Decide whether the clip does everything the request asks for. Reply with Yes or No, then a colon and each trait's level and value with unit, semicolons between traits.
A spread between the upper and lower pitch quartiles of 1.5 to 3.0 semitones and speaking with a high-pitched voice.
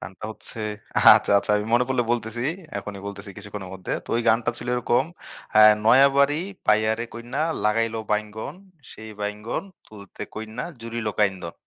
No: narrow, 2.5 semitones; low, 110 Hz